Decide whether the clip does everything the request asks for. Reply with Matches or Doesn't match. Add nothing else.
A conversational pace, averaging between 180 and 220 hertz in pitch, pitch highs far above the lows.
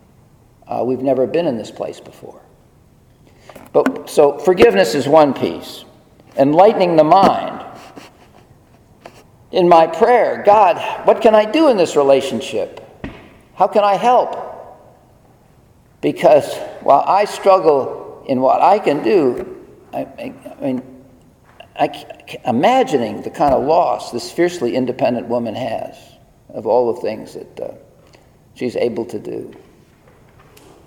Doesn't match